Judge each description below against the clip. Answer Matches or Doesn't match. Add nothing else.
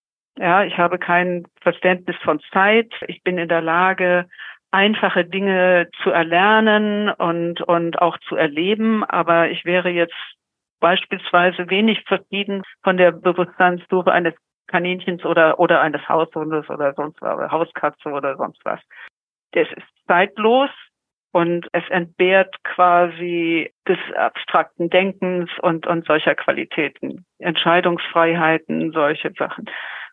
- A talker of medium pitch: Matches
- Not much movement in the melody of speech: Matches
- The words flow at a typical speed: Doesn't match